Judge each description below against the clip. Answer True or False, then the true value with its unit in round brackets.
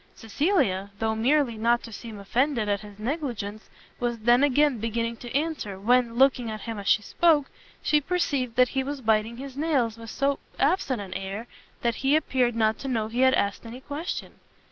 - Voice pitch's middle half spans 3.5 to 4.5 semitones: True (4.0 semitones)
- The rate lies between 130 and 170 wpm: False (190 wpm)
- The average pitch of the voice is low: False (240 Hz)